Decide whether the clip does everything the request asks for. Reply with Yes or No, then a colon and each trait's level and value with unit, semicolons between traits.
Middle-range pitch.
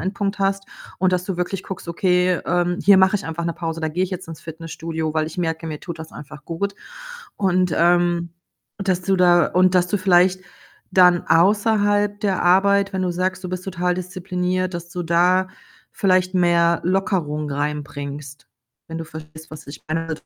Yes: medium, 180 Hz